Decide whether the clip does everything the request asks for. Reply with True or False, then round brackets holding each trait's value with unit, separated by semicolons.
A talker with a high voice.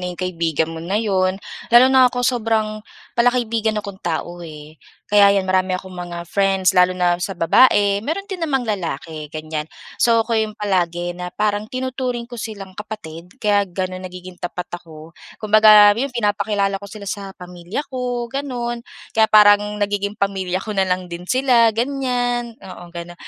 True (200 Hz)